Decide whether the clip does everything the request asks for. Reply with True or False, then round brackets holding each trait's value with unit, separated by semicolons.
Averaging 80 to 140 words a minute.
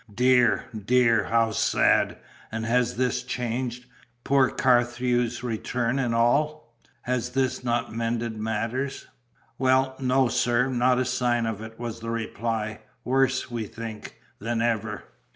True (135 wpm)